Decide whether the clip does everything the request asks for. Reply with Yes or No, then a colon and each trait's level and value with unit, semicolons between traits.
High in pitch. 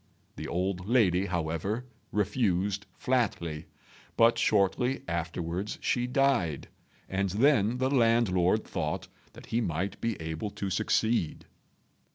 No: low, 100 Hz